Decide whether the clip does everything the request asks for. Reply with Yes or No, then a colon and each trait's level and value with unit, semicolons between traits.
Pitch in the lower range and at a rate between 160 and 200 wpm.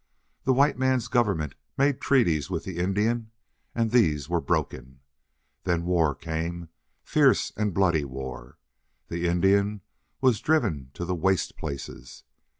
No: very low, 90 Hz; slow, 135 wpm